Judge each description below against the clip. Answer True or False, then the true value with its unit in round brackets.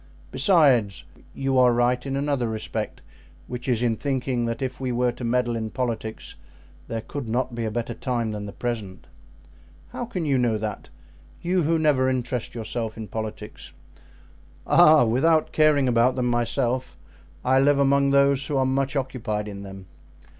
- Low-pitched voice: True (125 Hz)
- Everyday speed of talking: True (170 wpm)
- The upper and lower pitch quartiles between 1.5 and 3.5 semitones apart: True (3.2 semitones)